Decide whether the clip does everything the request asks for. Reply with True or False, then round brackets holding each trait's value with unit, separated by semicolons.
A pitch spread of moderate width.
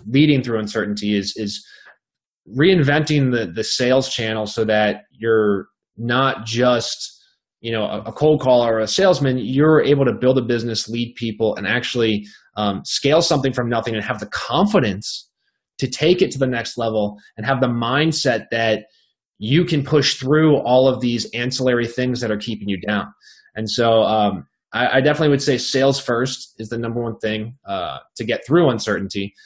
True (3.4 semitones)